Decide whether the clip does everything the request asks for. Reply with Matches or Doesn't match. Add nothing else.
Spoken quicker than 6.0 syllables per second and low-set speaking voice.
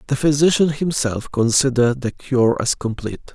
Doesn't match